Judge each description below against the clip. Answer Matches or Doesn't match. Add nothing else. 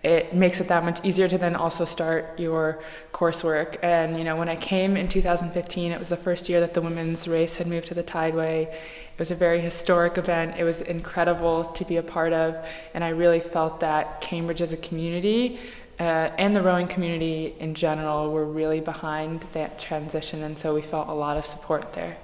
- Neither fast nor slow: Doesn't match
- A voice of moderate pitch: Matches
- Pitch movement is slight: Matches